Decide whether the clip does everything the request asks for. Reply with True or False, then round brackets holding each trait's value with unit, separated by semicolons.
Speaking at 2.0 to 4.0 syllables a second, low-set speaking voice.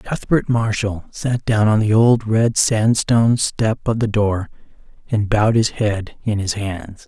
True (3.9 syllables/s; 110 Hz)